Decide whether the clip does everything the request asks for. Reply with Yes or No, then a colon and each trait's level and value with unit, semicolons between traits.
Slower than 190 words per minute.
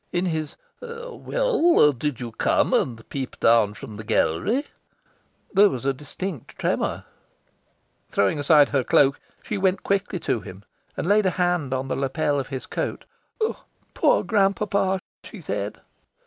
Yes: average, 150 wpm